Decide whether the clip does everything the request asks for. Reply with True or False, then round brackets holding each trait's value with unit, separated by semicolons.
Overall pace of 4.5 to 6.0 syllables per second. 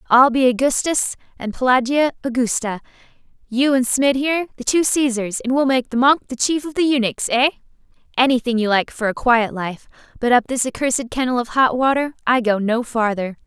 True (5.4 syllables/s)